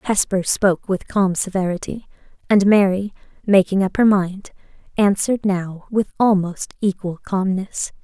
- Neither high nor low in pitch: No, high, 195 Hz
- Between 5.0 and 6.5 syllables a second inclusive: No, 4.5 syllables/s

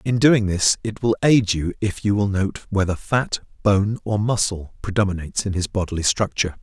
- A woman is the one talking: No, male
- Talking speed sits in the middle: Yes, average, 190 wpm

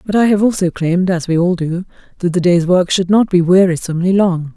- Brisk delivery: Yes, fast, 235 wpm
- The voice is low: No, medium, 180 Hz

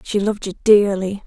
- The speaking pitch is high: Yes, high, 200 Hz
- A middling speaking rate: Yes, average, 190 wpm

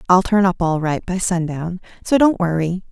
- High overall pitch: No, medium, 180 Hz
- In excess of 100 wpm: Yes, fast, 205 wpm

